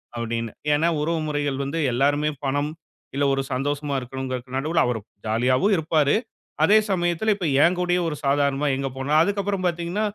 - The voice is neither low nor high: Yes, medium, 145 Hz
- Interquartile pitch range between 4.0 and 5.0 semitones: Yes, average, 4.3 semitones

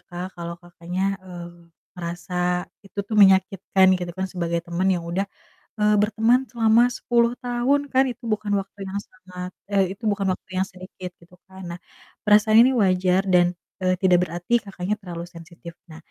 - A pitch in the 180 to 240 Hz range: Yes, high, 190 Hz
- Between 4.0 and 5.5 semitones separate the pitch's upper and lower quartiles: No, average, 2.9 semitones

